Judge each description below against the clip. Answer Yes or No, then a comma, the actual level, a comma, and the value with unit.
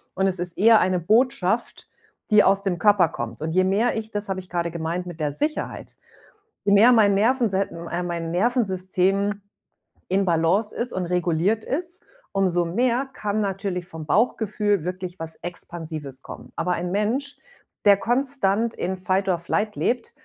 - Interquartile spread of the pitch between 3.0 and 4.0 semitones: Yes, average, 3.6 semitones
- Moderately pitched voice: No, high, 195 Hz